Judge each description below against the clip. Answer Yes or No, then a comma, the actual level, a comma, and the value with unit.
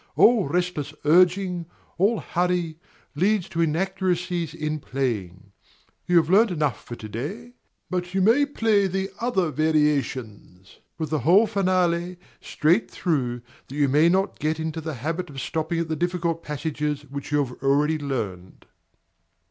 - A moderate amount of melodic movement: Yes, average, 4.1 semitones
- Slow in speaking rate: No, average, 150 wpm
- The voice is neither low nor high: Yes, medium, 160 Hz